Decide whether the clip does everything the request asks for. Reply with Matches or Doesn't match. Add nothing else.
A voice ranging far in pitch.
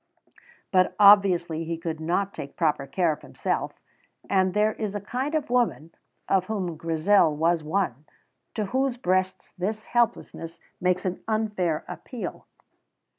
Doesn't match